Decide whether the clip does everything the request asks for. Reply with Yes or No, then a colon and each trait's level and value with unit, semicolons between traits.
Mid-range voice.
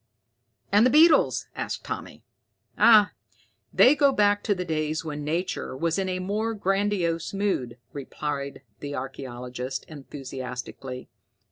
Yes: medium, 165 Hz